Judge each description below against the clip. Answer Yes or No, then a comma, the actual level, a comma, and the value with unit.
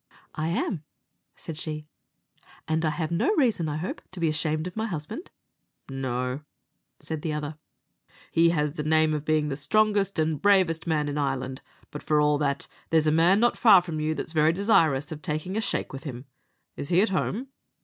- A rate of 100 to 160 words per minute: No, average, 195 wpm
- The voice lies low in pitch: No, medium, 155 Hz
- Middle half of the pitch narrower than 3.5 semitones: Yes, average, 3.0 semitones